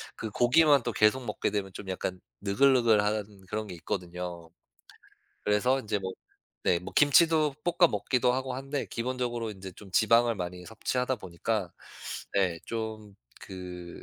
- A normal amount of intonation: Yes, average, 4.9 semitones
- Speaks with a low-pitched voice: Yes, low, 105 Hz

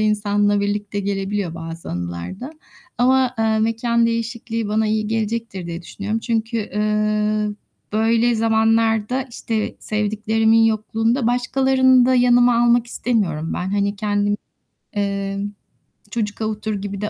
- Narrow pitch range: Yes, narrow, 2.1 semitones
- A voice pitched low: No, high, 215 Hz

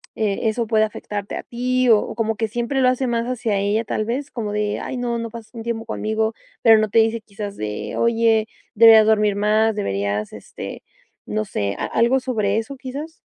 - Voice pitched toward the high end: Yes, high, 220 Hz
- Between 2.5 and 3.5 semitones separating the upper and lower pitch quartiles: No, narrow, 2.1 semitones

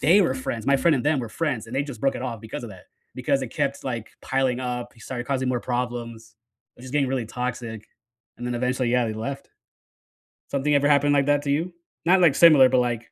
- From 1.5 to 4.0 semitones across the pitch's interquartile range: Yes, average, 2.8 semitones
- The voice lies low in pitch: Yes, low, 130 Hz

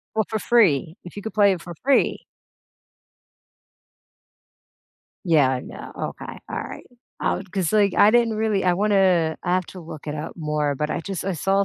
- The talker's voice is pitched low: No, medium, 185 Hz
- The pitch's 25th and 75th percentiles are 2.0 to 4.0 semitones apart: No, average, 4.4 semitones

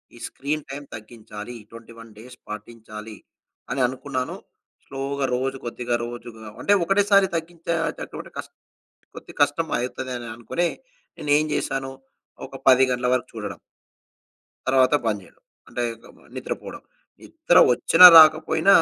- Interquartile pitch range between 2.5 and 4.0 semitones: No, average, 4.5 semitones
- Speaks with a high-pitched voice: No, low, 130 Hz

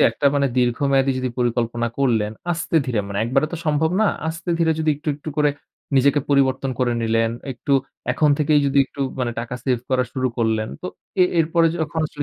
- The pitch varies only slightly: No, average, 4.0 semitones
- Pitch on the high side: No, low, 135 Hz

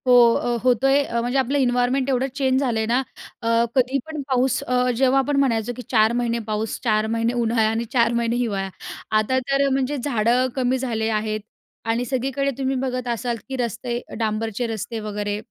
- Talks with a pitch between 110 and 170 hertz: No, high, 245 Hz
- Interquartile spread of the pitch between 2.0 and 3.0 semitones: Yes, narrow, 2.5 semitones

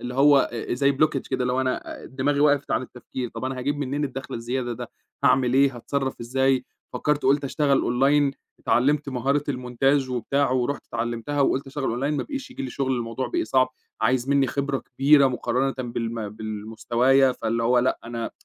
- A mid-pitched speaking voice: No, low, 130 Hz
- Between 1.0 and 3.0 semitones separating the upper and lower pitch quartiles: Yes, narrow, 2.4 semitones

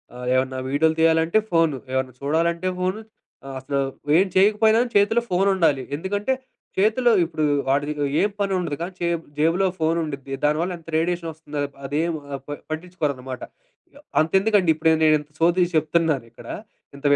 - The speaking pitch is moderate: Yes, medium, 165 Hz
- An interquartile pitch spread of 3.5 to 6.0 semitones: Yes, average, 4.2 semitones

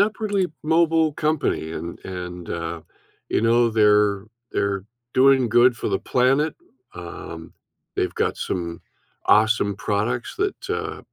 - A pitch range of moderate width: No, wide, 6.5 semitones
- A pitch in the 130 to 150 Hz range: No, low, 110 Hz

